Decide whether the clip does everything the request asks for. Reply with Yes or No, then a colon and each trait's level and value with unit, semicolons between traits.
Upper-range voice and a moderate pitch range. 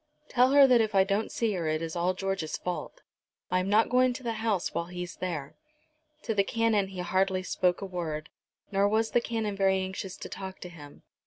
Yes: high, 195 Hz; average, 3.6 semitones